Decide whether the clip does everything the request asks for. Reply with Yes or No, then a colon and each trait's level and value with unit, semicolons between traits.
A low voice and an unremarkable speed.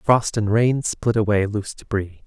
Yes: low, 105 Hz; average, 185 wpm